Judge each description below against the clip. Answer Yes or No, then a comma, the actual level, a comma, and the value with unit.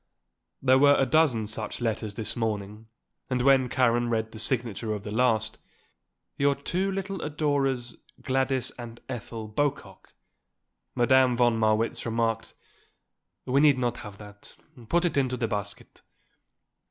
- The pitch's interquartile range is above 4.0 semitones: No, average, 3.4 semitones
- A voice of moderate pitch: No, low, 120 Hz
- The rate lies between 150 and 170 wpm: No, average, 140 wpm